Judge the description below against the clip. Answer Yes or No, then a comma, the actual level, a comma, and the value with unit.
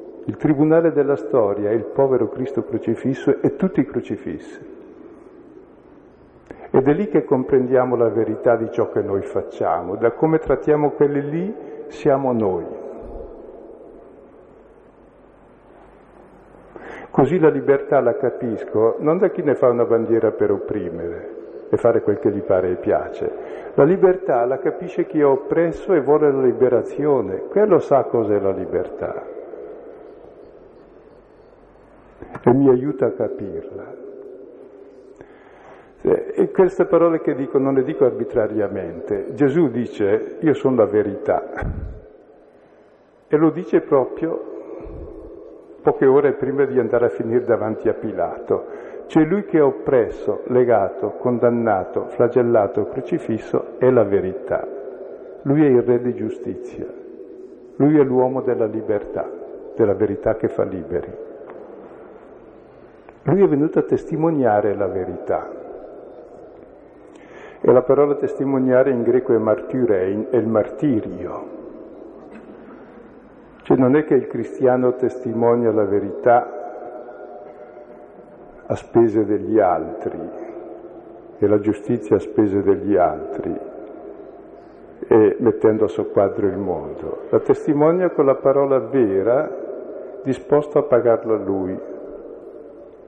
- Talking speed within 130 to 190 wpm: No, average, 120 wpm